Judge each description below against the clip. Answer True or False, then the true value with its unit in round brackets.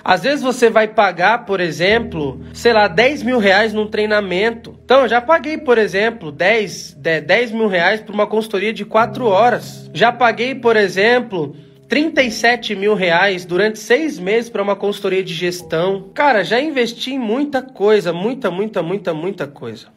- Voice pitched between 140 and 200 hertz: False (215 Hz)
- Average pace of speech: True (170 wpm)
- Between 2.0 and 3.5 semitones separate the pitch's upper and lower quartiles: False (3.9 semitones)